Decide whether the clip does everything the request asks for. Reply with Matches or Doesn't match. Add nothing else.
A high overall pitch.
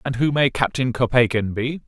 Doesn't match